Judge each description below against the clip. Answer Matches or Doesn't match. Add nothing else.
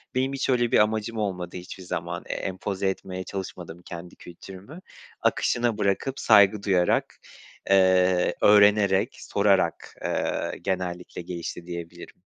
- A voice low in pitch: Matches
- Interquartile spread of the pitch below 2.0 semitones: Doesn't match